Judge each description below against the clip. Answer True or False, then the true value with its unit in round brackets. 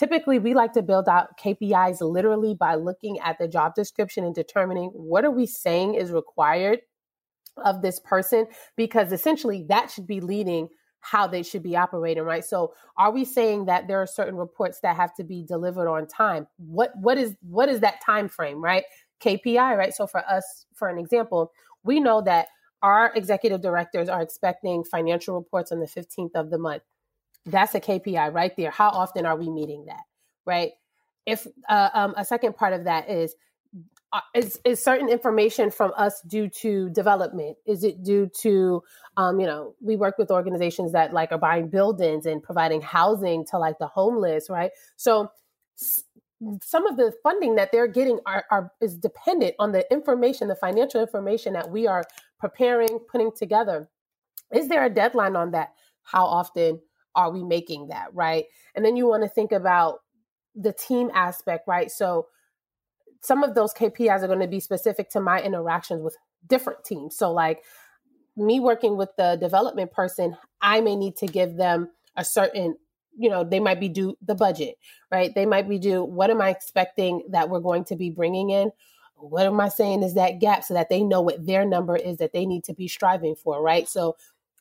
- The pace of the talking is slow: False (190 wpm)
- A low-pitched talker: False (195 Hz)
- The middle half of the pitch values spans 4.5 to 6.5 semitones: False (4.1 semitones)